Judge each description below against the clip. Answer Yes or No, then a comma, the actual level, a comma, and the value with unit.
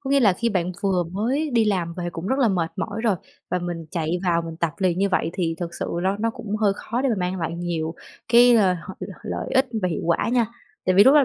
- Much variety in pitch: No, average, 4.7 semitones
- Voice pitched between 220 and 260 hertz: No, medium, 185 Hz